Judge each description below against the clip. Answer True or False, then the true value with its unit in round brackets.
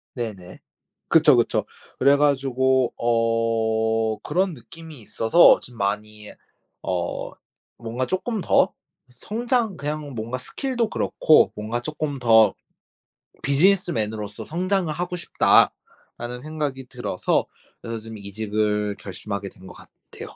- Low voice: True (120 Hz)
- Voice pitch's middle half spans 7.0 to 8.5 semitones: False (6.0 semitones)